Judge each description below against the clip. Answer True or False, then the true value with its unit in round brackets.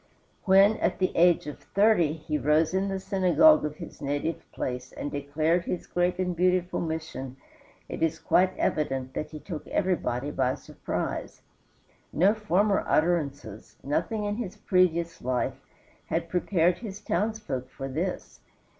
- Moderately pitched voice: True (170 Hz)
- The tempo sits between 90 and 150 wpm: True (145 wpm)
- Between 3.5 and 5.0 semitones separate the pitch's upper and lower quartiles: True (4.5 semitones)